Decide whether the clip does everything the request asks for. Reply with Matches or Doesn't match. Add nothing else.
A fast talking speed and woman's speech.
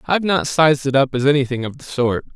Doesn't match